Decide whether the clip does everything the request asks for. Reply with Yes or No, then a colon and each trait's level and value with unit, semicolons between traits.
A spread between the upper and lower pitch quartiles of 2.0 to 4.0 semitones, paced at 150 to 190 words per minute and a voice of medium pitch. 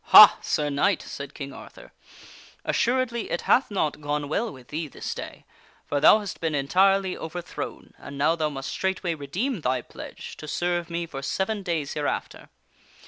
No: average, 4.9 semitones; average, 175 wpm; medium, 160 Hz